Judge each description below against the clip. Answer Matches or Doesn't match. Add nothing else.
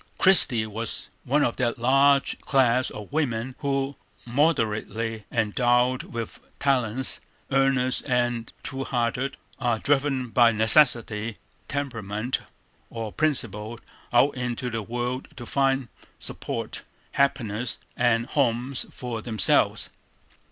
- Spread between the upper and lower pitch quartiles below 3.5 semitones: Matches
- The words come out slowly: Matches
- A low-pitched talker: Matches